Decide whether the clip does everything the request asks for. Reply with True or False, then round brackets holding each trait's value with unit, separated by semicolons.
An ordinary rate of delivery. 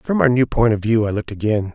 False (310 wpm)